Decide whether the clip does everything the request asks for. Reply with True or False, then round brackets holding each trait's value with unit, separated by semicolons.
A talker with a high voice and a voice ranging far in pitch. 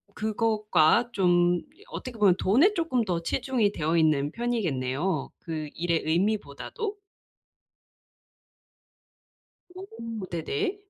True (200 Hz; 6.4 semitones)